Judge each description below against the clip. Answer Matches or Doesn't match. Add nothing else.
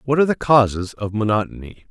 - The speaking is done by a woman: Doesn't match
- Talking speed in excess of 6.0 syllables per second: Matches